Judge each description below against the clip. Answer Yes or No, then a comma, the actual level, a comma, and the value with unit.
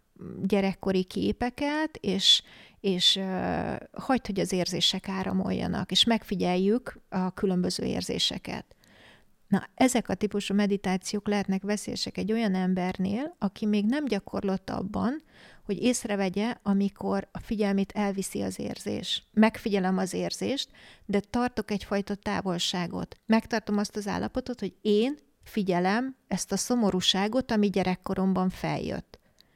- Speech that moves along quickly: No, average, 120 wpm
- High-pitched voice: Yes, high, 200 Hz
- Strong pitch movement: No, narrow, 2.6 semitones